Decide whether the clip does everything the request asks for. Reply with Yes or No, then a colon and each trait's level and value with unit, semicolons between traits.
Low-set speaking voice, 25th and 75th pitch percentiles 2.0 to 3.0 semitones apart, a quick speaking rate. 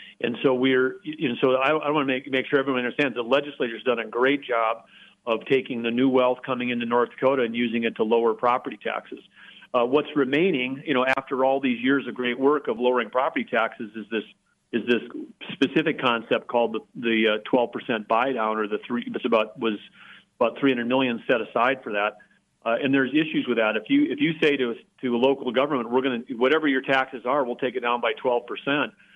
Yes: low, 130 Hz; narrow, 2.4 semitones; fast, 220 wpm